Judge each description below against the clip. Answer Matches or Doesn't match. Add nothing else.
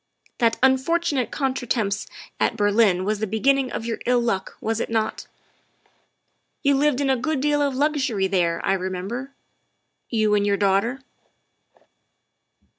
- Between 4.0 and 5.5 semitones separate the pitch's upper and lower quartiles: Matches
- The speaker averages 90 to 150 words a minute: Matches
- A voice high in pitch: Matches